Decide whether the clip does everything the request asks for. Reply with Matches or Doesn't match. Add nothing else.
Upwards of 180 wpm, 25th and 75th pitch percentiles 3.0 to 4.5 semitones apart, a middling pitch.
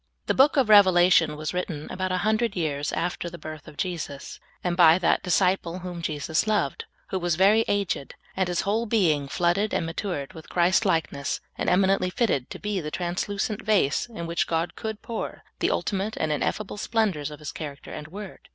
Matches